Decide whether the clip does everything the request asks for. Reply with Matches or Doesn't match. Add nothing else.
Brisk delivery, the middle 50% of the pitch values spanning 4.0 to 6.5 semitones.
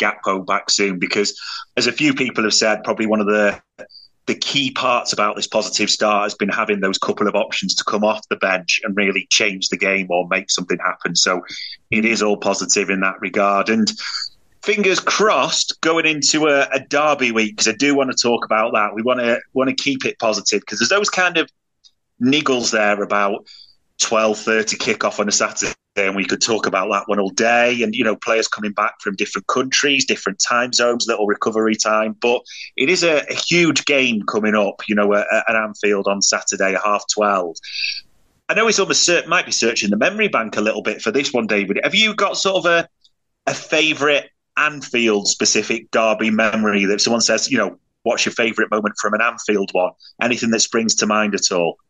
Matches